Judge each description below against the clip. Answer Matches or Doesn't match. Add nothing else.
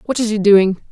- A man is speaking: Doesn't match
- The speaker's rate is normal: Doesn't match